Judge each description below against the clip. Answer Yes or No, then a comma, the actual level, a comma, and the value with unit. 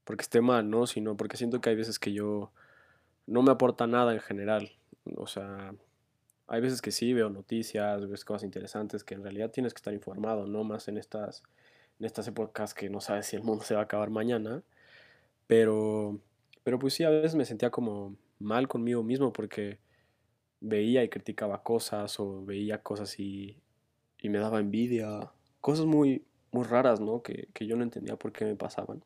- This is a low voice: Yes, low, 110 Hz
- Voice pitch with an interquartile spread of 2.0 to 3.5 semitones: Yes, narrow, 2.6 semitones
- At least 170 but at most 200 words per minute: Yes, fast, 190 wpm